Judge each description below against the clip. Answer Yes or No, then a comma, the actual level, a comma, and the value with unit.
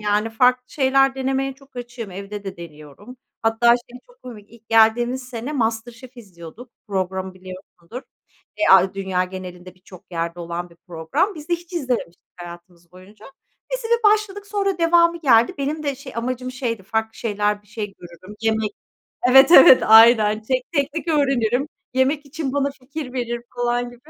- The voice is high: Yes, high, 235 Hz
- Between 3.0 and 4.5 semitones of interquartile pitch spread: No, wide, 5.6 semitones